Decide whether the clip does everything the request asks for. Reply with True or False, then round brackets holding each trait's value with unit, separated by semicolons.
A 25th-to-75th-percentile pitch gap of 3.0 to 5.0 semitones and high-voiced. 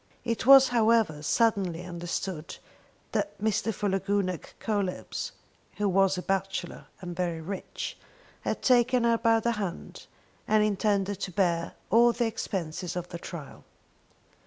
True (4.0 semitones; 195 Hz)